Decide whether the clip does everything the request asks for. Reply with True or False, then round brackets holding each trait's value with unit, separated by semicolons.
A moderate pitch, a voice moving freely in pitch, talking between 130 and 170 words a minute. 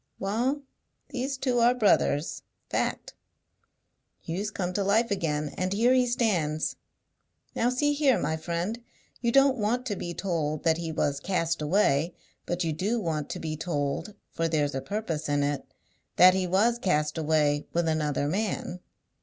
True (180 Hz; 6.4 semitones; 160 wpm)